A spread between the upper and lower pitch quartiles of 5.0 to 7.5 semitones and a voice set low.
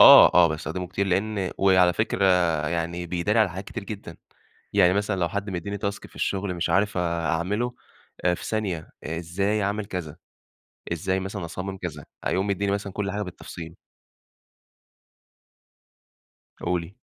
No: average, 2.7 semitones; very low, 95 Hz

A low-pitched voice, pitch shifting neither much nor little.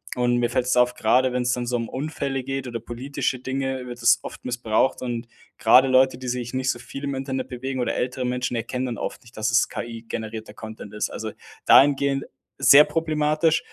No: low, 125 Hz; narrow, 1.8 semitones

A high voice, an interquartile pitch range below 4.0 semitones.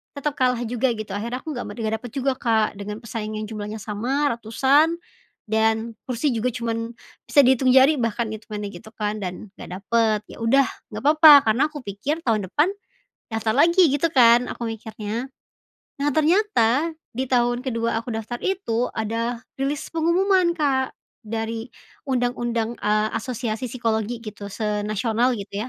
Yes: high, 235 Hz; average, 3.3 semitones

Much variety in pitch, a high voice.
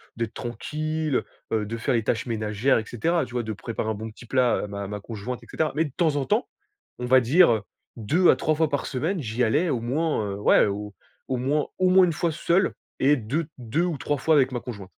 No: wide, 5.8 semitones; low, 125 Hz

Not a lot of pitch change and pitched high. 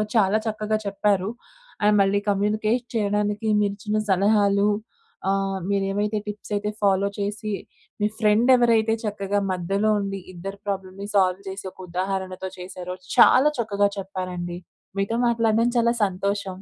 Yes: narrow, 1.7 semitones; high, 200 Hz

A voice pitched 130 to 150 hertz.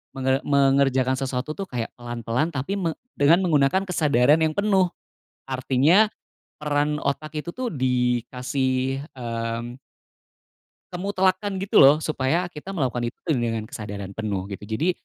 Yes: low, 135 Hz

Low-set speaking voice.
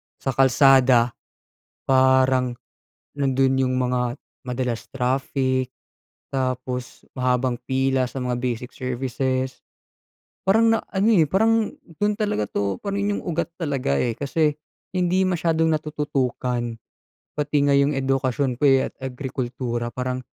Yes: low, 130 Hz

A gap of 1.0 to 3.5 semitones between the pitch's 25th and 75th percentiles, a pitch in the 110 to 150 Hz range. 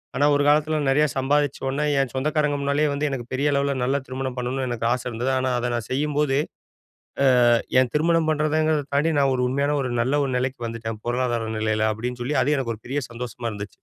Yes: average, 3.1 semitones; low, 135 Hz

